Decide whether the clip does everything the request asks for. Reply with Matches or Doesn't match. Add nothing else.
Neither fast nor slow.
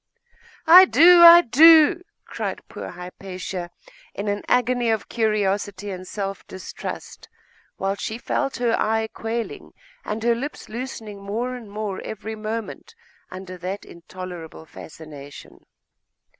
Doesn't match